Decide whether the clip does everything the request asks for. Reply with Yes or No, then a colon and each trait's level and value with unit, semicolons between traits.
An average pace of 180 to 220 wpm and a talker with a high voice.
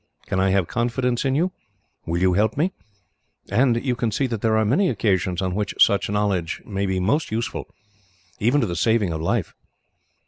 No: average, 195 wpm; low, 110 Hz